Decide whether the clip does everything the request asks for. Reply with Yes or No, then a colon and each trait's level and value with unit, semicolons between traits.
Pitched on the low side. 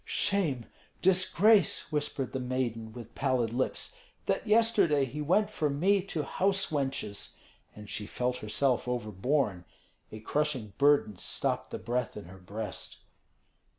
Yes: low, 130 Hz